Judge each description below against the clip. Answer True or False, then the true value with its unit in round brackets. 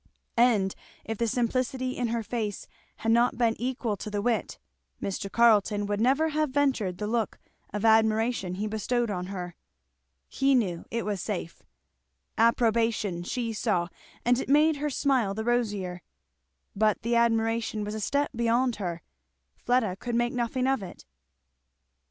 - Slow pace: False (155 wpm)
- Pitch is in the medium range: False (225 Hz)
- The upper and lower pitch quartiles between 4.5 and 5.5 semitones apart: False (2.9 semitones)